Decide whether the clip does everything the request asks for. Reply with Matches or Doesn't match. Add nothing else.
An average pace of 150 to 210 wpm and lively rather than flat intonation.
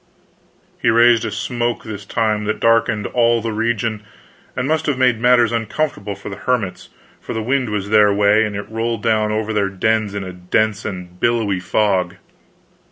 Doesn't match